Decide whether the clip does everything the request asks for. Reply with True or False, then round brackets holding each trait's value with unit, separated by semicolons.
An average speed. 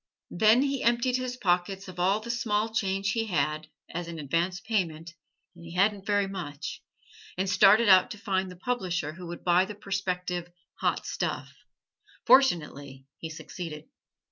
True (160 wpm)